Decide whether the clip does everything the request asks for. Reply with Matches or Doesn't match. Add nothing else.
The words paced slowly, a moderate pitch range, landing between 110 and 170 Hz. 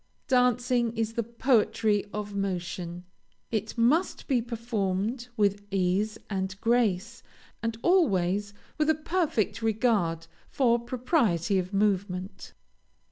Doesn't match